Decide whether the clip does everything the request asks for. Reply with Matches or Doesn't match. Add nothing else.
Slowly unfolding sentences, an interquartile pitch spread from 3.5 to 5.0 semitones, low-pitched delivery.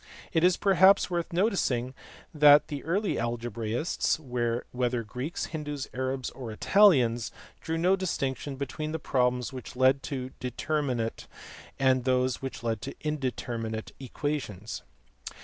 Matches